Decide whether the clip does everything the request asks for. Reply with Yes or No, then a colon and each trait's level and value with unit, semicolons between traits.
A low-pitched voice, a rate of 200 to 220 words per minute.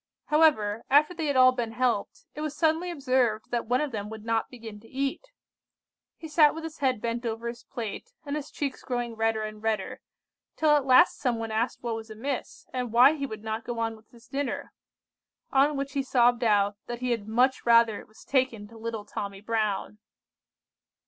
No: high, 240 Hz; fast, 205 wpm